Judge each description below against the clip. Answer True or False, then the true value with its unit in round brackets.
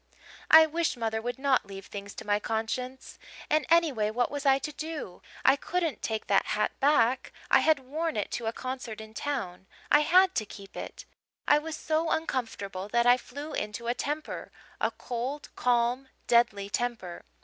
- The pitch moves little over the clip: False (5.3 semitones)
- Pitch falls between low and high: False (250 Hz)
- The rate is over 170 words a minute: True (180 wpm)